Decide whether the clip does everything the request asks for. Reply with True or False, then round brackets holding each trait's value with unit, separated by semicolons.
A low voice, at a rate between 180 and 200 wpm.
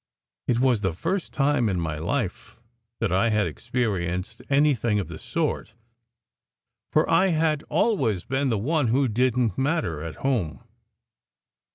False (120 Hz; 150 wpm)